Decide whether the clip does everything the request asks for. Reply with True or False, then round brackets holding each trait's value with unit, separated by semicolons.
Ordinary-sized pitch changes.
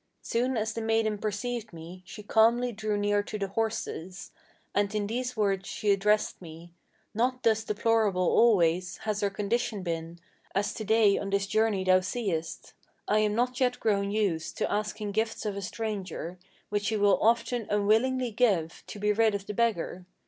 False (2.3 semitones)